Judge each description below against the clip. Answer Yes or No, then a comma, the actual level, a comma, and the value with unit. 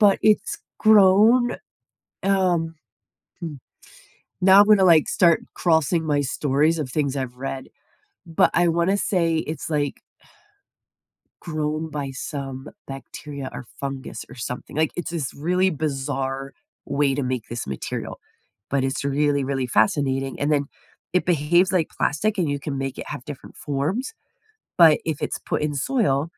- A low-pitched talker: No, medium, 150 Hz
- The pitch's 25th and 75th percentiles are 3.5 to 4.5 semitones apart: Yes, average, 4.2 semitones